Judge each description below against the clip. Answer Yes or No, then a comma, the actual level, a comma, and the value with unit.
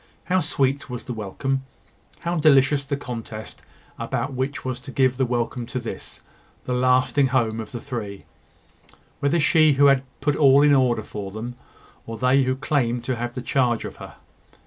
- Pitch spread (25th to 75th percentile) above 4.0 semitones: No, average, 2.7 semitones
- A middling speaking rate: Yes, average, 180 wpm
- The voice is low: Yes, low, 130 Hz